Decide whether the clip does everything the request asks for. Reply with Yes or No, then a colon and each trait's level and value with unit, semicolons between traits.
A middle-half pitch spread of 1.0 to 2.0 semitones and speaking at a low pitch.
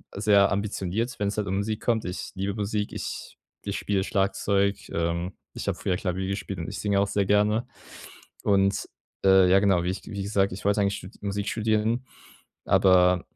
Yes: narrow, 1.4 semitones; low, 100 Hz